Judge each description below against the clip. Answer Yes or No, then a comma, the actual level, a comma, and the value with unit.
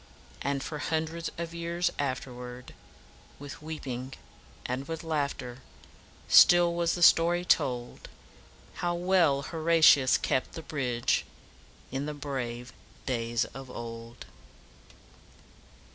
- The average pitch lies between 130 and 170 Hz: Yes, medium, 140 Hz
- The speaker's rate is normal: No, slow, 110 wpm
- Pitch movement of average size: Yes, average, 4.8 semitones